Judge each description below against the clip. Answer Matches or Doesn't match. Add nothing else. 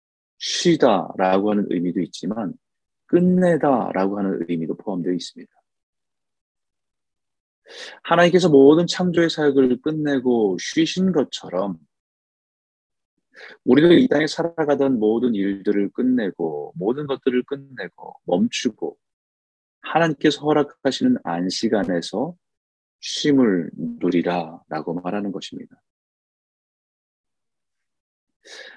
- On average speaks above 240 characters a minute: Doesn't match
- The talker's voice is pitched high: Doesn't match